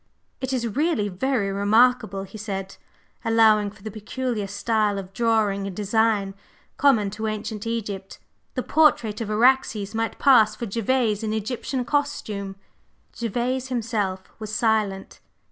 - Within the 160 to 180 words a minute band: No, slow, 135 wpm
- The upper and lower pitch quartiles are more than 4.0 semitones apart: No, average, 2.9 semitones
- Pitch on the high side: Yes, high, 220 Hz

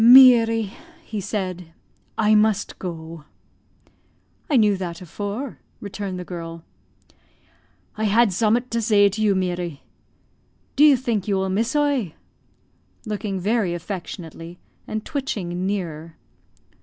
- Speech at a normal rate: No, slow, 120 wpm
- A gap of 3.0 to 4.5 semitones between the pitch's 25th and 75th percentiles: Yes, average, 4.1 semitones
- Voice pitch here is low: No, high, 200 Hz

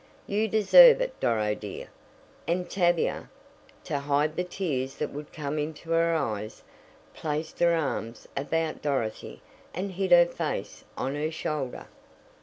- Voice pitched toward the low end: No, medium, 155 Hz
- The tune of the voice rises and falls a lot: No, average, 3.8 semitones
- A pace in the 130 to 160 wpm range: Yes, average, 140 wpm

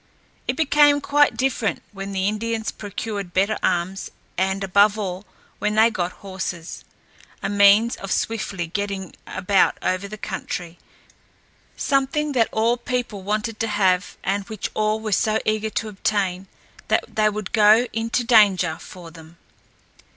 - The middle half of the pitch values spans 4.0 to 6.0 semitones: No, average, 2.7 semitones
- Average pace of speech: Yes, average, 145 wpm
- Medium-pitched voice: No, high, 205 Hz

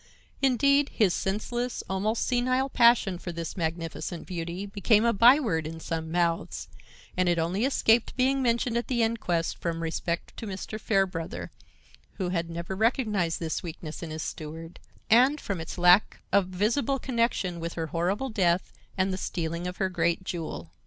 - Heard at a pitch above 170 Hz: Yes, medium, 185 Hz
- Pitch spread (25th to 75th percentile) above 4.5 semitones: Yes, wide, 5.6 semitones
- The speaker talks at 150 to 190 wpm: Yes, average, 165 wpm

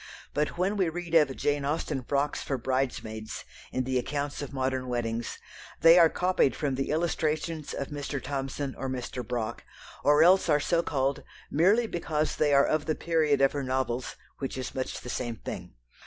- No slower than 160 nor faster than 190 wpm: Yes, average, 185 wpm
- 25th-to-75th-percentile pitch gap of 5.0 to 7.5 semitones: No, average, 3.3 semitones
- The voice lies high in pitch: No, medium, 140 Hz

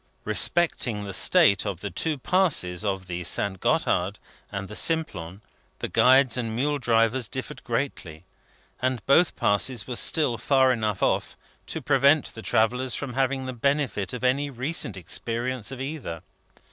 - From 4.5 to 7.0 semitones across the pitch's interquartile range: Yes, average, 4.9 semitones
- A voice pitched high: No, low, 120 Hz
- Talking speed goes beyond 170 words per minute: No, average, 155 wpm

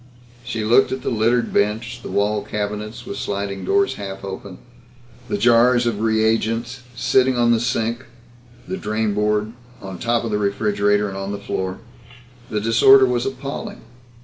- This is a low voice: Yes, low, 110 Hz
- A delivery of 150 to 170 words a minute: Yes, average, 155 wpm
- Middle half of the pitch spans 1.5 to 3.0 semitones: Yes, average, 2.7 semitones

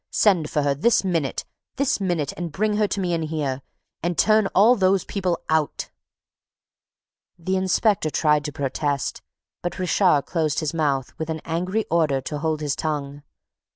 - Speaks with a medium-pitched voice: Yes, medium, 165 Hz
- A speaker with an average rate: Yes, average, 165 wpm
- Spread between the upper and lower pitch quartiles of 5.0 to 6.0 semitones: No, average, 4.1 semitones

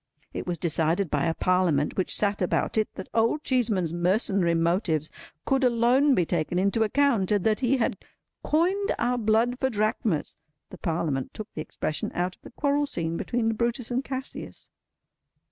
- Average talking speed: Yes, average, 170 wpm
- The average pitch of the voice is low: No, high, 210 Hz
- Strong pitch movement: Yes, wide, 6.1 semitones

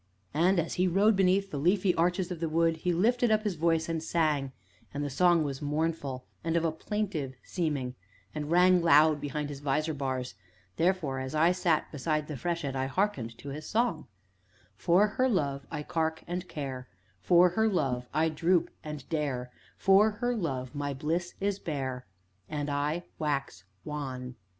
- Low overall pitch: No, medium, 160 Hz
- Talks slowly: No, average, 175 wpm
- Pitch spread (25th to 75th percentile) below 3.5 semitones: No, average, 4.0 semitones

